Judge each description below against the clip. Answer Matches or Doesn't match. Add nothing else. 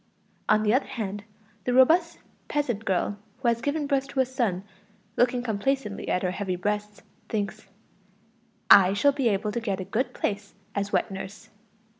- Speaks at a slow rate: Doesn't match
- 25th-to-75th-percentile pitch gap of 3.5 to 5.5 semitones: Matches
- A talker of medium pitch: Doesn't match